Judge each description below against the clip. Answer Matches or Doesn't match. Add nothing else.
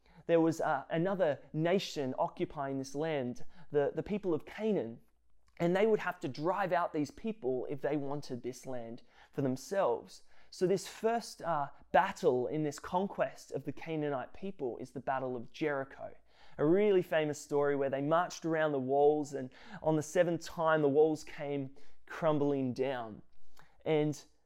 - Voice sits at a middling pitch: Matches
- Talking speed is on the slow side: Doesn't match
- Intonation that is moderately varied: Matches